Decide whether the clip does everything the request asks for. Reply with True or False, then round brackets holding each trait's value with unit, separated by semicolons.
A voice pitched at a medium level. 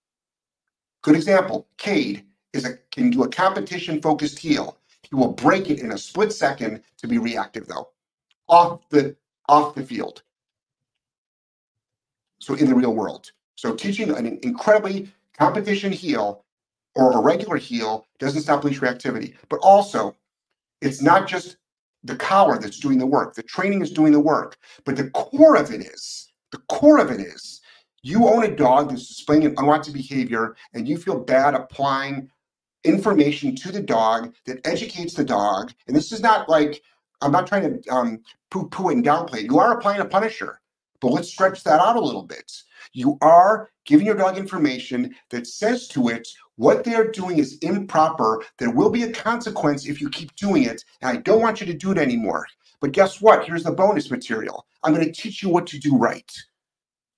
True (165 Hz)